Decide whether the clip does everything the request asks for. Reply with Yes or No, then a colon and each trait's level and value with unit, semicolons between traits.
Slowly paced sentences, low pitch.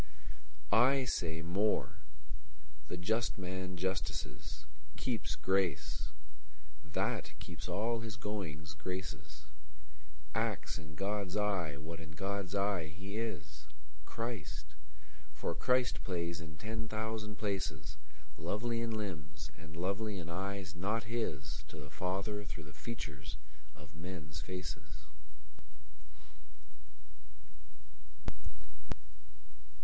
Yes: slow, 90 wpm; very low, 95 Hz